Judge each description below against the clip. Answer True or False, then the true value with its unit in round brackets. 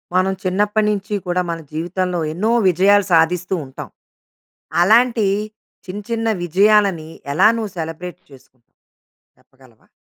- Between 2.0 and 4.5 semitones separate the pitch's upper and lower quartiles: True (4.0 semitones)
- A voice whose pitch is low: False (185 Hz)